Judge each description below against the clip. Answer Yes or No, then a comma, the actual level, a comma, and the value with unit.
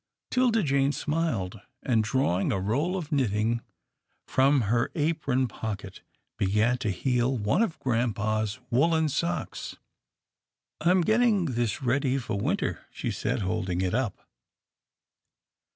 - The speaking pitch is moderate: No, low, 125 Hz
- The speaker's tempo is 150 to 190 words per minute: No, slow, 135 wpm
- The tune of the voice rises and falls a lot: Yes, wide, 6.0 semitones